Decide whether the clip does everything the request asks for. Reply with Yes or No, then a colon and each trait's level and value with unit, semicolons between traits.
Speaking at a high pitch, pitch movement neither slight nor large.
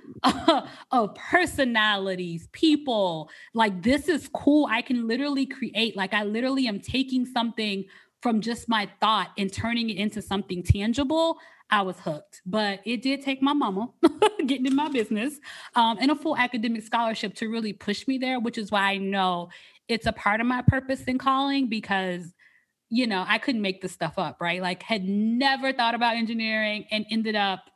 Yes: high, 225 Hz; average, 4.7 semitones